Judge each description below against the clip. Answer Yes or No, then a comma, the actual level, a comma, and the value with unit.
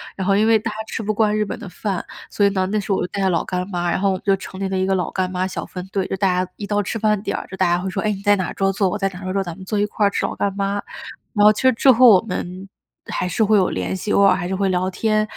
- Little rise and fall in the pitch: Yes, narrow, 1.9 semitones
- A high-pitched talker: Yes, high, 195 Hz